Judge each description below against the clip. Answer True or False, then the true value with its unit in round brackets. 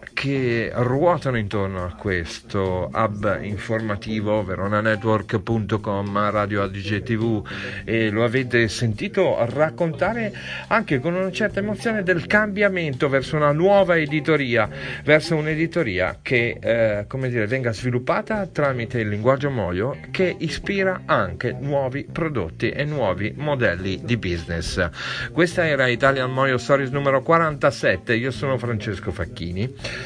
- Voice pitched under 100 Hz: False (125 Hz)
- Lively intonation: True (6.2 semitones)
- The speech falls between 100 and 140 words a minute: True (120 wpm)